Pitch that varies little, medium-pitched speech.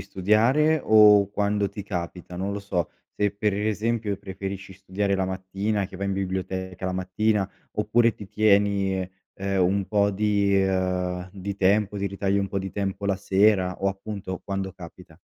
No: narrow, 1.5 semitones; low, 100 Hz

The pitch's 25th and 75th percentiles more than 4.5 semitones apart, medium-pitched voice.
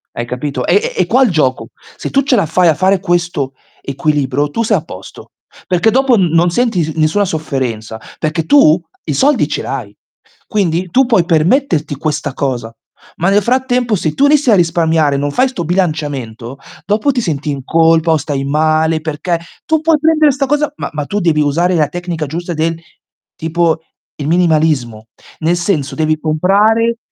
Yes: wide, 5.5 semitones; medium, 165 Hz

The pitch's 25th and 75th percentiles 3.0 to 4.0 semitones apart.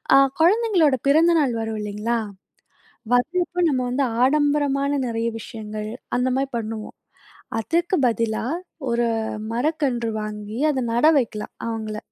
No: average, 4.8 semitones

